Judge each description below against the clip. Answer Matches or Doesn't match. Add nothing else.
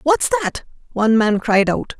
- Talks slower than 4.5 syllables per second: Doesn't match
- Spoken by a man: Doesn't match